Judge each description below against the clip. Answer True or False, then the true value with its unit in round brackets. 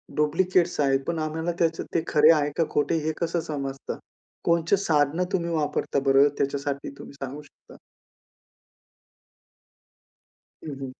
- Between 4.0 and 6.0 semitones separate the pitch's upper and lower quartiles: False (2.8 semitones)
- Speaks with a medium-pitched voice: True (150 Hz)